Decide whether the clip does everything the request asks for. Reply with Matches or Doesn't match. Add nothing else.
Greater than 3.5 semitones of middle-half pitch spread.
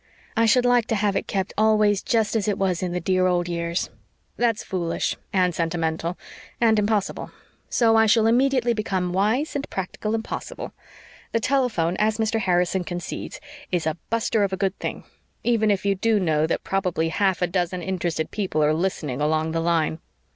Matches